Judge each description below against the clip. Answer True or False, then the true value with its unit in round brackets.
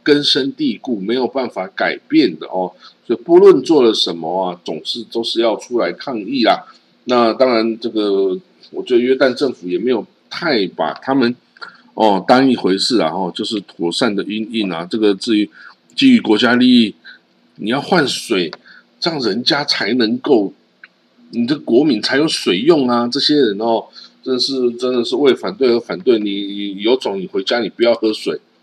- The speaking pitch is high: False (120 Hz)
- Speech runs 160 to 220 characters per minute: False (255 characters per minute)